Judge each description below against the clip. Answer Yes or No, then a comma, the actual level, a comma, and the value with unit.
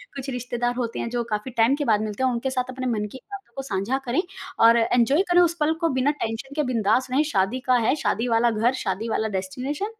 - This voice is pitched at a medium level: No, high, 245 Hz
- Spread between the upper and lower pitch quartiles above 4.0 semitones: No, average, 2.9 semitones